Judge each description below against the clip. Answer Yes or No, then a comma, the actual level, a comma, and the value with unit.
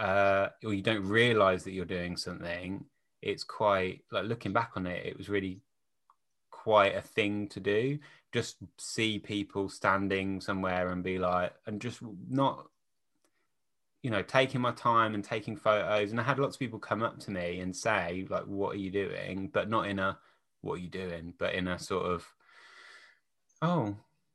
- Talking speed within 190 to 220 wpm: No, average, 180 wpm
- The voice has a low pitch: Yes, low, 100 Hz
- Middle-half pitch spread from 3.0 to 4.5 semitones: Yes, average, 3.5 semitones